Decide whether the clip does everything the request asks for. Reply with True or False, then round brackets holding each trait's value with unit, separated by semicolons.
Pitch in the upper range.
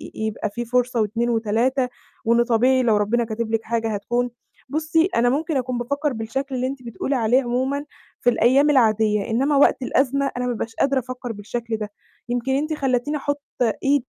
True (245 Hz)